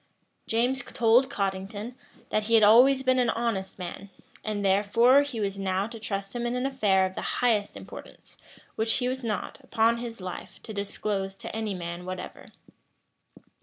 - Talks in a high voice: Yes, high, 220 Hz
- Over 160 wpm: Yes, average, 170 wpm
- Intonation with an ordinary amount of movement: Yes, average, 3.6 semitones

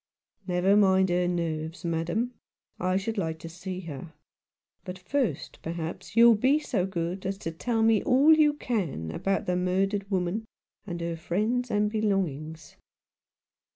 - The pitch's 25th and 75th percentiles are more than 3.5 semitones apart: Yes, average, 4.2 semitones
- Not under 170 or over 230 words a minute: No, average, 155 wpm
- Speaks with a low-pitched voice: No, medium, 185 Hz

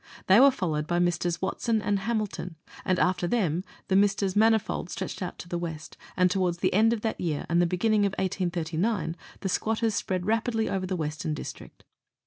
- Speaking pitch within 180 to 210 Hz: Yes, medium, 185 Hz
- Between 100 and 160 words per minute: No, average, 190 wpm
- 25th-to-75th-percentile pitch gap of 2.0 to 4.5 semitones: Yes, average, 3.7 semitones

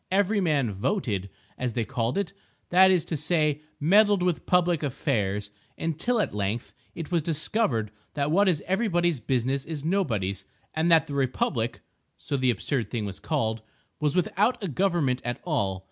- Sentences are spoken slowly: No, average, 160 wpm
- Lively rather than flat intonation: Yes, wide, 7.2 semitones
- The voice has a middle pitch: Yes, medium, 150 Hz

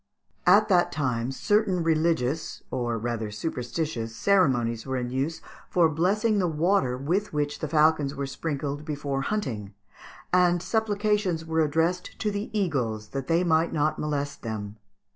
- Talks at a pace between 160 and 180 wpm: No, average, 150 wpm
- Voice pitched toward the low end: No, medium, 155 Hz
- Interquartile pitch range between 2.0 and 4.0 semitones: No, wide, 5.6 semitones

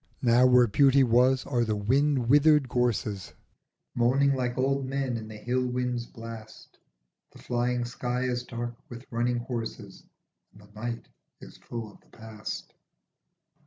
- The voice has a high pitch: No, low, 120 Hz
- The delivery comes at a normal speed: Yes, average, 150 wpm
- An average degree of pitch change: No, narrow, 1.8 semitones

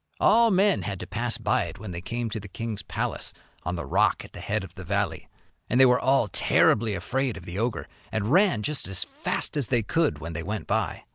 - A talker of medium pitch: No, low, 110 Hz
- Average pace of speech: No, fast, 235 wpm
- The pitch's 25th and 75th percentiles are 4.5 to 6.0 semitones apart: Yes, average, 5.0 semitones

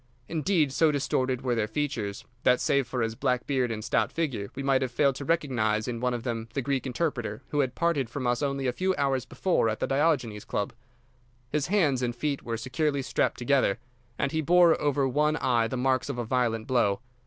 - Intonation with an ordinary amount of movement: Yes, average, 3.4 semitones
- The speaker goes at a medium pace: No, fast, 215 wpm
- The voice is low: Yes, low, 130 Hz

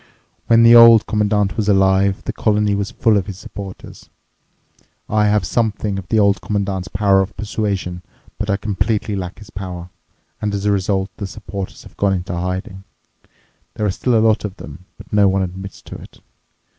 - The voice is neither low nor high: No, low, 100 Hz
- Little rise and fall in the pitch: Yes, narrow, 1.7 semitones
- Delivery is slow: No, average, 185 wpm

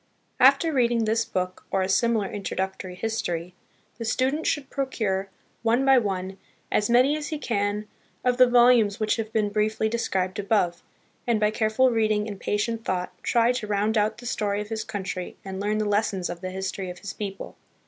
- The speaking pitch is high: Yes, high, 215 Hz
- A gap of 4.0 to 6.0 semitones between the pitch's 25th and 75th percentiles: No, average, 3.3 semitones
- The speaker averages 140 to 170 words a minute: No, average, 195 wpm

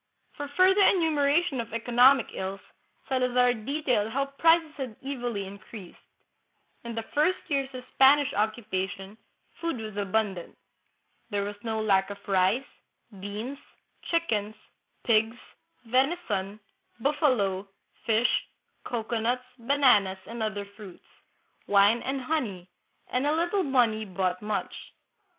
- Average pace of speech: No, slow, 120 wpm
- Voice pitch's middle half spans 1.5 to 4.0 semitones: No, average, 5.2 semitones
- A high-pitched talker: Yes, high, 235 Hz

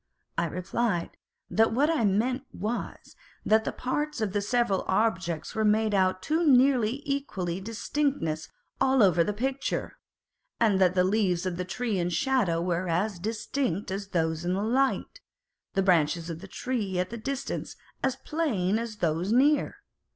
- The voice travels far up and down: Yes, wide, 5.7 semitones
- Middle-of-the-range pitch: No, high, 210 Hz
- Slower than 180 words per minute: Yes, average, 165 wpm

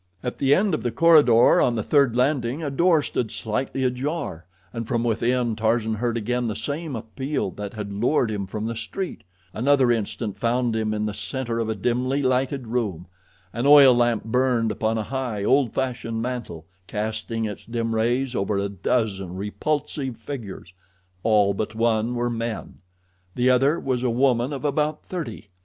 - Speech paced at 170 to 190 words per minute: Yes, average, 175 wpm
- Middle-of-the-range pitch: No, low, 120 Hz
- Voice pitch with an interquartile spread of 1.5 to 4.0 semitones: Yes, average, 3.2 semitones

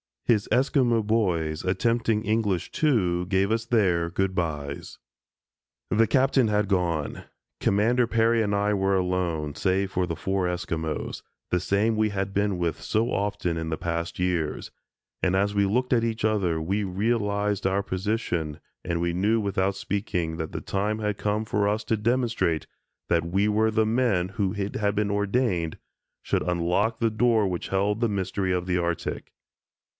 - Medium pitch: No, low, 100 Hz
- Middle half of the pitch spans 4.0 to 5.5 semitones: No, average, 3.5 semitones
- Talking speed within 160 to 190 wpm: Yes, average, 170 wpm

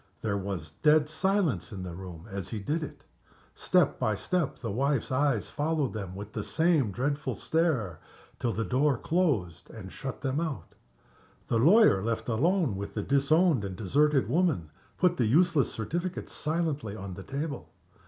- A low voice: Yes, low, 130 Hz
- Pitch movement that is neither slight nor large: No, wide, 7.5 semitones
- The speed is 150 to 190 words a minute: Yes, average, 165 wpm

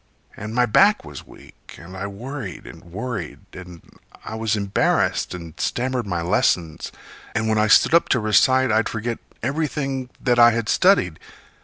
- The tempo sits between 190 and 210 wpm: No, average, 165 wpm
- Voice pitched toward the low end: Yes, low, 110 Hz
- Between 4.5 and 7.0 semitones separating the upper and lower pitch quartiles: Yes, average, 5.2 semitones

